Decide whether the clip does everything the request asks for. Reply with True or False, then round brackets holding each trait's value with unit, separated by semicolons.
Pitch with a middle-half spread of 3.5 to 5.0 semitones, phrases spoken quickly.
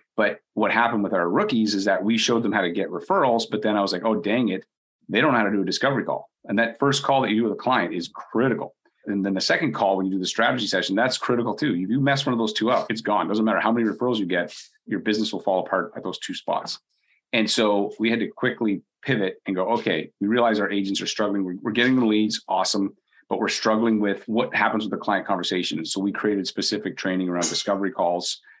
False (2.5 semitones; 260 wpm)